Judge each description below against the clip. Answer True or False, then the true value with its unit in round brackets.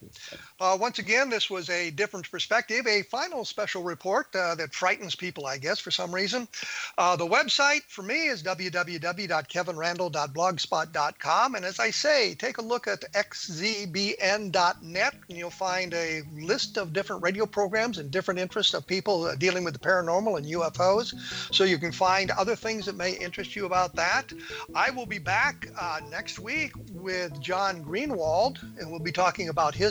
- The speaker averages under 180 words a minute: True (170 wpm)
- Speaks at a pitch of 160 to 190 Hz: True (185 Hz)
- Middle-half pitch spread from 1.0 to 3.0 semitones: True (2.7 semitones)